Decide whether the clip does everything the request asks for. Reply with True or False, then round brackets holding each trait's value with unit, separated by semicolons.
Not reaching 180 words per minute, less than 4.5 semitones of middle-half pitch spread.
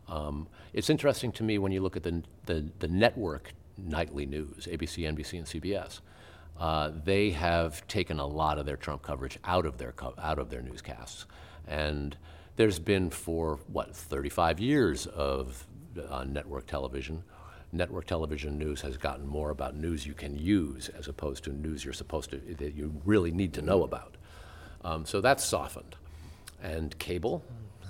True (170 wpm; 3.4 semitones)